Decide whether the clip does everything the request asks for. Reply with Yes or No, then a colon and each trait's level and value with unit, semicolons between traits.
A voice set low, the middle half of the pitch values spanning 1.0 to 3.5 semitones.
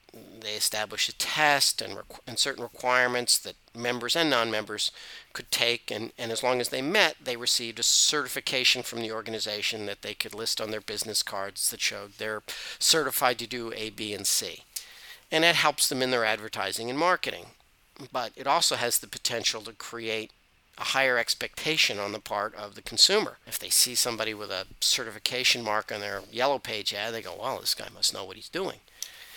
Yes: low, 120 Hz; narrow, 2.5 semitones